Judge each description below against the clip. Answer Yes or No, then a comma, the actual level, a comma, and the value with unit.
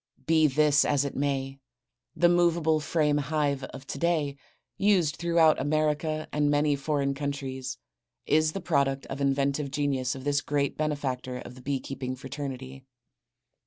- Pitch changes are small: Yes, narrow, 2.1 semitones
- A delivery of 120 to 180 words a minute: Yes, average, 150 wpm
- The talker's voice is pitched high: No, medium, 145 Hz